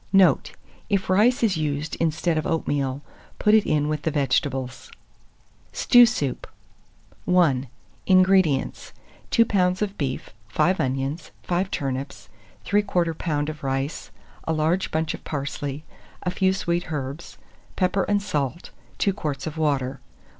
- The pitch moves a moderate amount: Yes, average, 4.8 semitones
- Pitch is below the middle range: No, medium, 155 Hz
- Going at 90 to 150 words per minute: Yes, average, 140 wpm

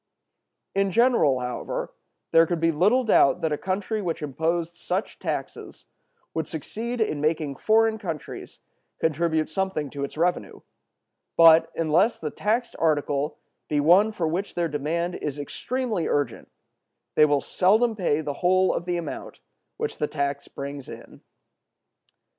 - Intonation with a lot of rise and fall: No, average, 4.7 semitones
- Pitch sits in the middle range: Yes, medium, 165 Hz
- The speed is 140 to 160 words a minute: Yes, average, 145 wpm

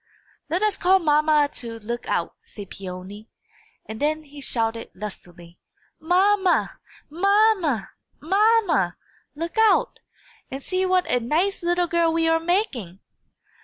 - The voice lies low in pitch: No, very high, 315 Hz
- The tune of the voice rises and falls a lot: Yes, wide, 8.3 semitones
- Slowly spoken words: Yes, slow, 130 wpm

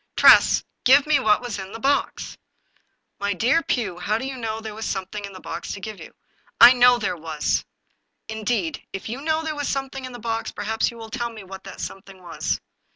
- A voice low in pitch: No, high, 225 Hz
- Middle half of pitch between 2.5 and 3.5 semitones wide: No, average, 4.4 semitones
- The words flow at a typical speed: No, fast, 260 wpm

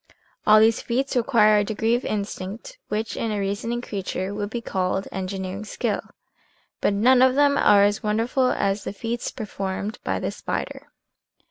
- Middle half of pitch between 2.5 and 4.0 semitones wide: Yes, average, 3.0 semitones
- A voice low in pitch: No, high, 215 Hz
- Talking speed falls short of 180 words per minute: Yes, average, 165 wpm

